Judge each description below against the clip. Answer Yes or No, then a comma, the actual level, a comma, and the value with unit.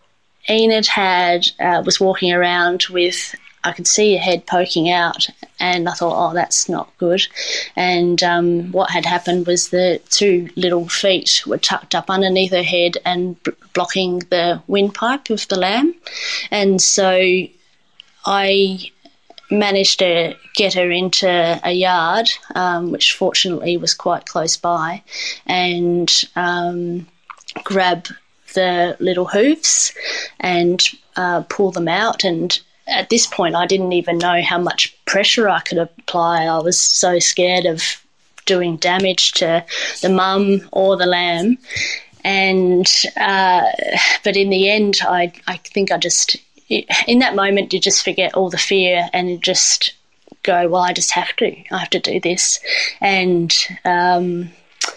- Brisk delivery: No, average, 145 wpm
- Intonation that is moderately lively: No, narrow, 1.9 semitones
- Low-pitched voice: No, medium, 180 Hz